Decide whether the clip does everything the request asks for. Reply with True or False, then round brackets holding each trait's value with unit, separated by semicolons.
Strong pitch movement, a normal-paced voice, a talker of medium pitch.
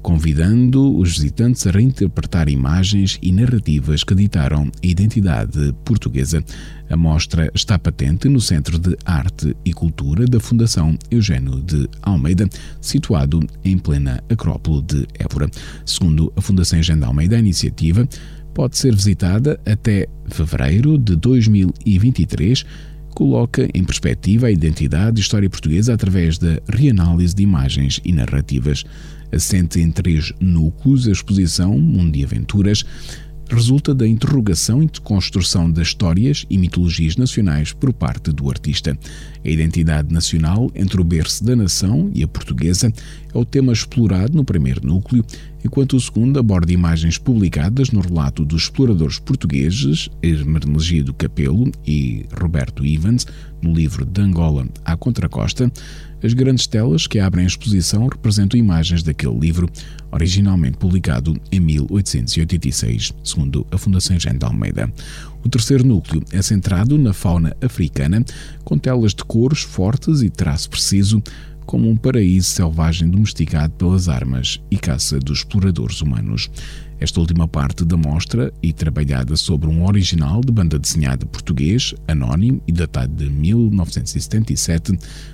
False (6.6 semitones; 140 wpm; 90 Hz)